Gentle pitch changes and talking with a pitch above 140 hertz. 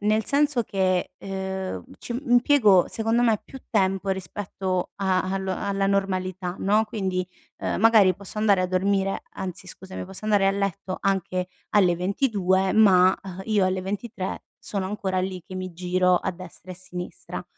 Yes: narrow, 1.8 semitones; high, 190 Hz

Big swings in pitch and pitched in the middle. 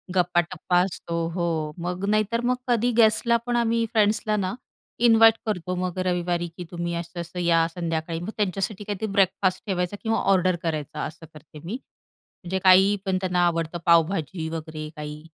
No: average, 3.4 semitones; medium, 180 Hz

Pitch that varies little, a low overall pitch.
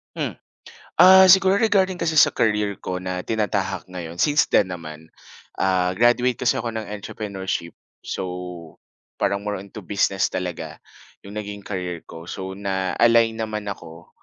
No: average, 3.7 semitones; low, 100 Hz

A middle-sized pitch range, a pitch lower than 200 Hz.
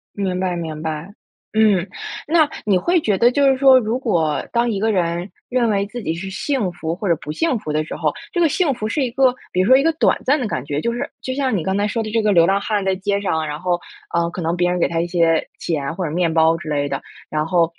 No: wide, 5.9 semitones; high, 190 Hz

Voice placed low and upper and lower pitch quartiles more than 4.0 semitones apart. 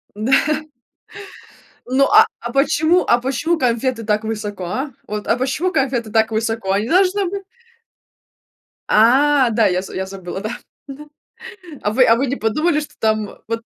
No: high, 235 Hz; average, 4.5 semitones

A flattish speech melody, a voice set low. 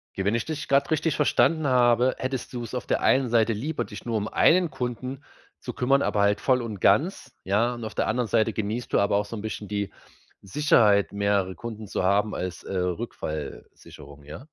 No: average, 4.0 semitones; low, 115 Hz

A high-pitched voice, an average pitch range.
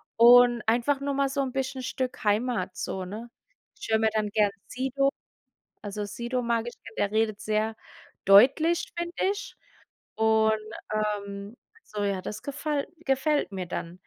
Yes: high, 225 Hz; average, 4.3 semitones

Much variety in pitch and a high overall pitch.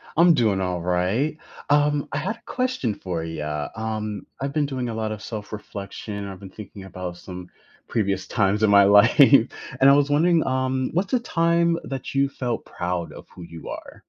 No: wide, 6.7 semitones; low, 110 Hz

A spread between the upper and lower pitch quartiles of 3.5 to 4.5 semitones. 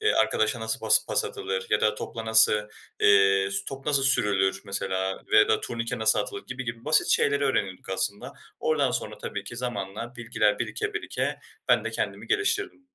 No: wide, 5.4 semitones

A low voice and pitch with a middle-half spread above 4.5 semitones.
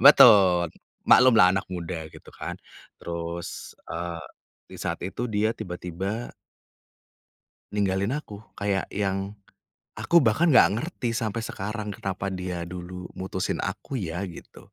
No: very low, 95 Hz; average, 3.6 semitones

